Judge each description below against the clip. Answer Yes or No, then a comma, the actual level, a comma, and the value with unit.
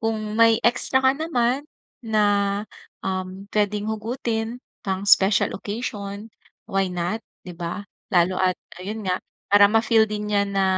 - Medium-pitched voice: No, high, 205 Hz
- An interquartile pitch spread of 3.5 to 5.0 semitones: No, narrow, 2.6 semitones